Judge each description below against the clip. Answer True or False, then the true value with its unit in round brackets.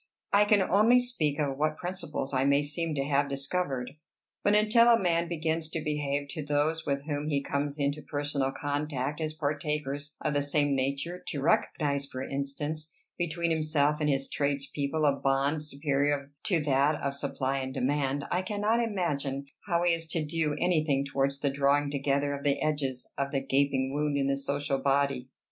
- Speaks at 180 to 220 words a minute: True (185 wpm)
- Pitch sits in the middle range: True (145 Hz)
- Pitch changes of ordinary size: False (2.2 semitones)